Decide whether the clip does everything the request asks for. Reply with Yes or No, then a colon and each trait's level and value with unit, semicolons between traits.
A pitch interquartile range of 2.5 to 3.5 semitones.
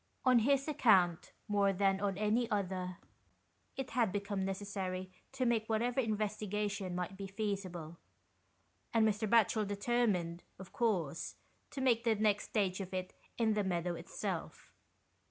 Yes: average, 3.1 semitones